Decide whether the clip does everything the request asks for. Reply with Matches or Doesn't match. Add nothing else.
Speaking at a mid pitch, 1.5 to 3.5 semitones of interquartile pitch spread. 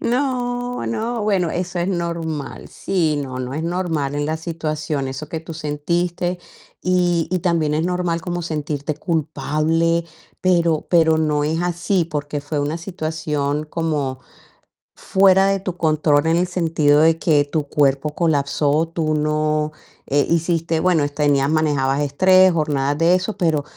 Matches